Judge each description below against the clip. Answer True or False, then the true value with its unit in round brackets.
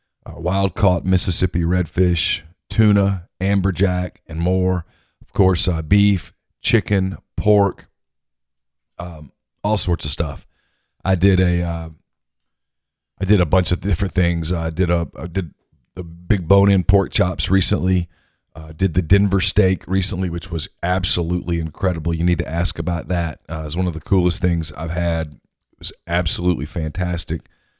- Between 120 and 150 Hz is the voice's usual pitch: False (90 Hz)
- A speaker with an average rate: True (160 wpm)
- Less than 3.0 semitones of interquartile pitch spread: True (2.4 semitones)